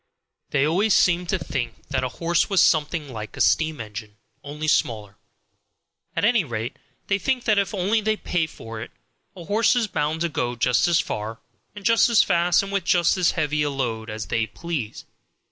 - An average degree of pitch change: No, wide, 7.7 semitones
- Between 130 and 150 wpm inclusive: No, average, 195 wpm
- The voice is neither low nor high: Yes, medium, 160 Hz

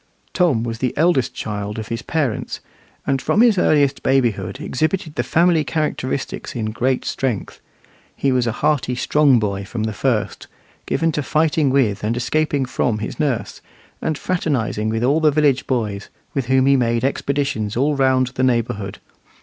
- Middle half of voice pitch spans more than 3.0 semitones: Yes, average, 4.6 semitones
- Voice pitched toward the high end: No, low, 130 Hz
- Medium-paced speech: Yes, average, 165 wpm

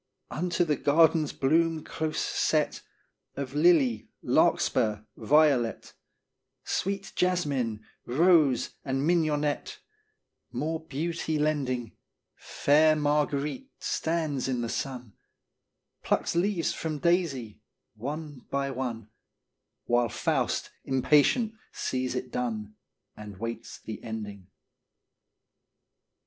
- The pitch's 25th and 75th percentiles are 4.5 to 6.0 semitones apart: Yes, average, 4.8 semitones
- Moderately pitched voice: Yes, medium, 145 Hz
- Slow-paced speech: Yes, slow, 95 wpm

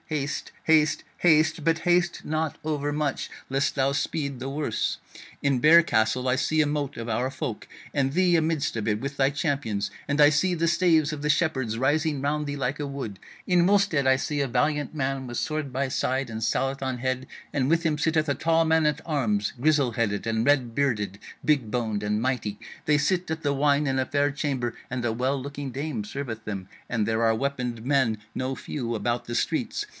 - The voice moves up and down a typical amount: Yes, average, 3.8 semitones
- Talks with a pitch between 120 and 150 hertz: Yes, medium, 140 Hz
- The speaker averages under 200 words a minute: No, fast, 205 wpm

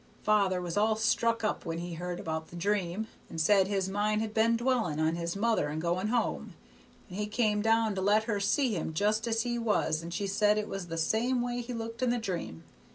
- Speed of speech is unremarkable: No, fast, 230 wpm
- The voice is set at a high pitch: Yes, high, 210 Hz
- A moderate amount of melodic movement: Yes, average, 4.3 semitones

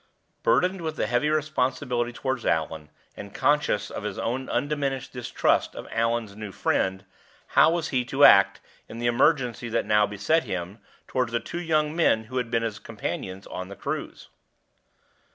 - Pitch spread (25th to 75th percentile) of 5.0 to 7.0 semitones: Yes, wide, 5.5 semitones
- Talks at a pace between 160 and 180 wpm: Yes, average, 170 wpm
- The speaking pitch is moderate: No, low, 120 Hz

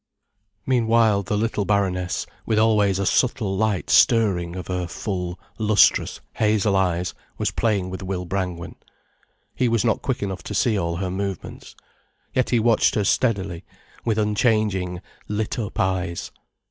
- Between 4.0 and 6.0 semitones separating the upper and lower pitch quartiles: No, average, 3.1 semitones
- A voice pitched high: No, low, 100 Hz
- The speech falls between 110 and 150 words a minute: Yes, average, 145 wpm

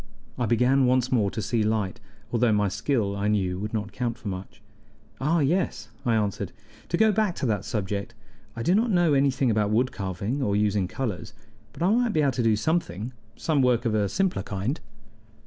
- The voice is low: Yes, low, 115 Hz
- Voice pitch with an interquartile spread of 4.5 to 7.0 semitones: Yes, average, 5.0 semitones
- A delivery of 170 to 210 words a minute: Yes, average, 200 wpm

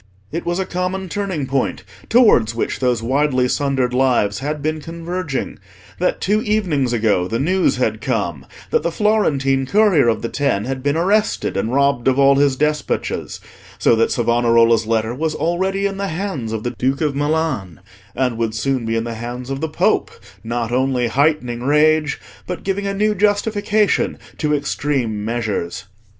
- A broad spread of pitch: Yes, wide, 6.4 semitones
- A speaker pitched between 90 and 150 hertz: Yes, medium, 140 Hz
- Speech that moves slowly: No, average, 170 wpm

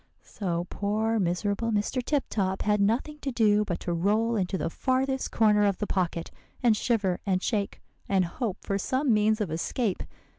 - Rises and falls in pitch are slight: No, average, 3.3 semitones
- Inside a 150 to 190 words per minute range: Yes, average, 180 wpm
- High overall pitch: Yes, high, 210 Hz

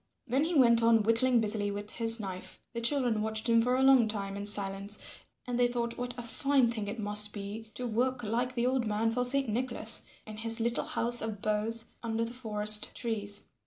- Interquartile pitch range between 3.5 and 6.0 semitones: No, narrow, 2.5 semitones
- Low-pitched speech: No, high, 230 Hz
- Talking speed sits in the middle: No, fast, 210 wpm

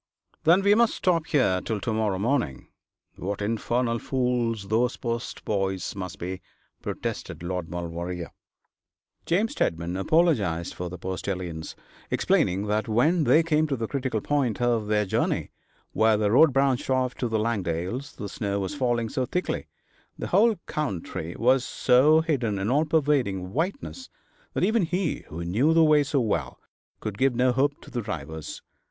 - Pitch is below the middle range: Yes, low, 115 Hz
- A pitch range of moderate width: No, wide, 7.0 semitones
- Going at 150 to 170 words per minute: Yes, average, 160 wpm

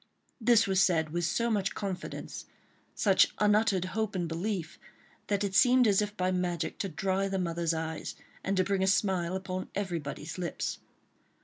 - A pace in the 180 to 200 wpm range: No, average, 170 wpm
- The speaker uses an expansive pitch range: No, average, 2.9 semitones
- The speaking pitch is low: No, high, 190 Hz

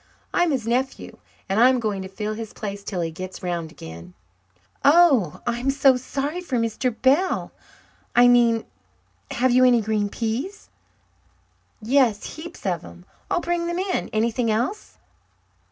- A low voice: No, high, 235 Hz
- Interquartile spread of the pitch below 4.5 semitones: No, average, 4.9 semitones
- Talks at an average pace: Yes, average, 150 wpm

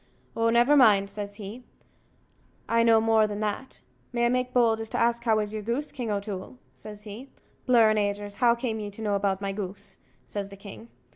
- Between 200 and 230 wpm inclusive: Yes, fast, 205 wpm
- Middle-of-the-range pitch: No, high, 220 Hz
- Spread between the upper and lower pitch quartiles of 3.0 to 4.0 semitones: No, narrow, 2.5 semitones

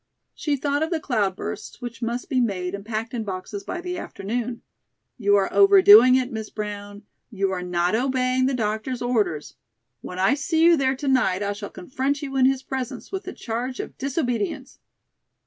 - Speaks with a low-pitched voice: No, high, 245 Hz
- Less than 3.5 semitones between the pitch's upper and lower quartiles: No, average, 4.8 semitones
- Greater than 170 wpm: Yes, average, 190 wpm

